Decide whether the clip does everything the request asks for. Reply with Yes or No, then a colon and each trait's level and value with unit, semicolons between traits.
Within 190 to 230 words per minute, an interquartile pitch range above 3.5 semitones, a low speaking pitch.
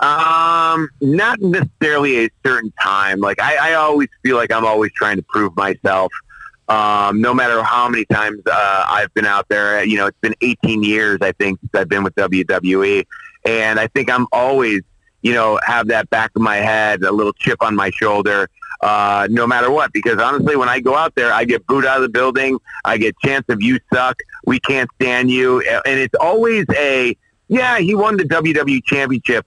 Yes: average, 200 wpm; average, 5.1 semitones; low, 125 Hz